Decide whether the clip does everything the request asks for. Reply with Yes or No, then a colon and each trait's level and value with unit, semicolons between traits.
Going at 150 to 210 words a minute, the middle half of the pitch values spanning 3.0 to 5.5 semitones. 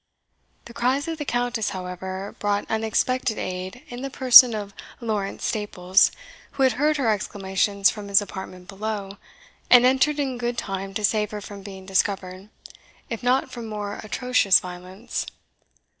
Yes: average, 155 wpm; average, 4.1 semitones